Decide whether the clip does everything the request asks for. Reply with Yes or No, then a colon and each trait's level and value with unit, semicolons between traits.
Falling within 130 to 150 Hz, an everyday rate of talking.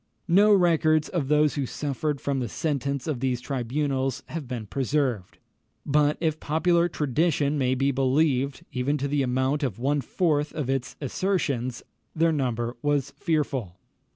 Yes: medium, 140 Hz; average, 155 wpm